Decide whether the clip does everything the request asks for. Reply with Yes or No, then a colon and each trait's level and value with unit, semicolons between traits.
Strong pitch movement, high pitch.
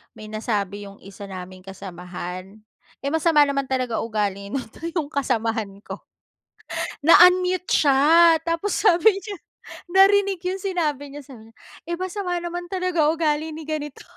Yes: wide, 8.6 semitones; very high, 290 Hz